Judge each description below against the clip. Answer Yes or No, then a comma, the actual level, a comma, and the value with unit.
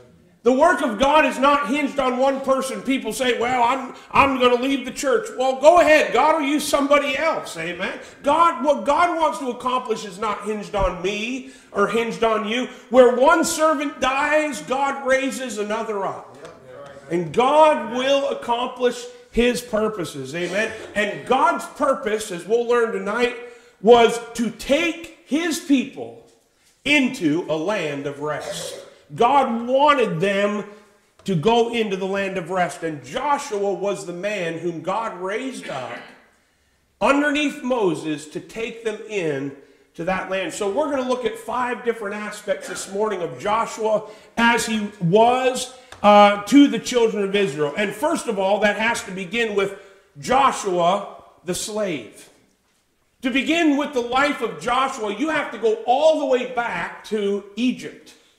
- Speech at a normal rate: Yes, average, 160 wpm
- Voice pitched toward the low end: No, high, 235 Hz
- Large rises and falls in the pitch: No, average, 4.9 semitones